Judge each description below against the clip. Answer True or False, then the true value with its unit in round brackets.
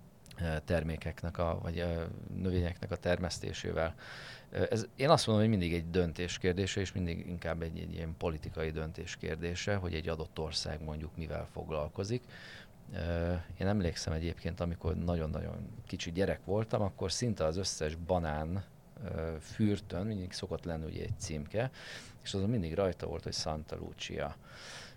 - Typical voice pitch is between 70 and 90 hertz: True (85 Hz)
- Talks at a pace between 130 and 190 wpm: True (145 wpm)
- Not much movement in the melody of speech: False (3.5 semitones)